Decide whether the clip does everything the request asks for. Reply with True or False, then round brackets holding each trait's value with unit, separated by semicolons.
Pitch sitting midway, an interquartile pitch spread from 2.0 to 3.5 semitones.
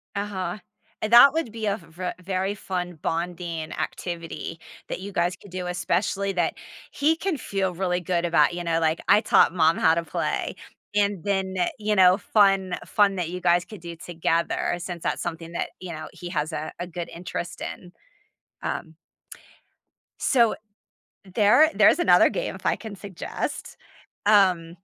True (180 Hz; 2.9 semitones)